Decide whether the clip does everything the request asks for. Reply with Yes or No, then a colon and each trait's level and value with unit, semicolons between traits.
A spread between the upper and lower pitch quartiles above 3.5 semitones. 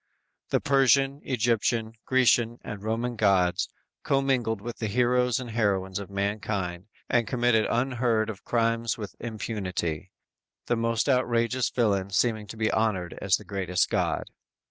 No: average, 3.2 semitones